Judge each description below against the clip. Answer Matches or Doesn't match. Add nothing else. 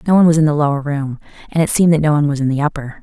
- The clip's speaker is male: Doesn't match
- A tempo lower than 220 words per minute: Doesn't match